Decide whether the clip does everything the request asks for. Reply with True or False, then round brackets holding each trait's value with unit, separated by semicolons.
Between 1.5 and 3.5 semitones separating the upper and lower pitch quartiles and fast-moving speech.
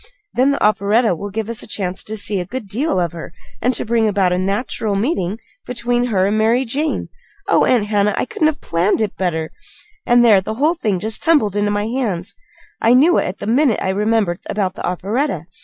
False (4.0 semitones; 220 wpm)